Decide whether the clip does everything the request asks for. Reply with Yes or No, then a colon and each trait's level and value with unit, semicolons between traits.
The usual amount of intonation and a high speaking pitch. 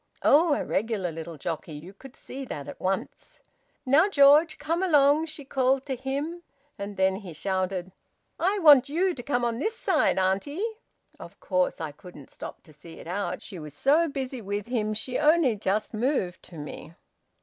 No: wide, 7.8 semitones; high, 240 Hz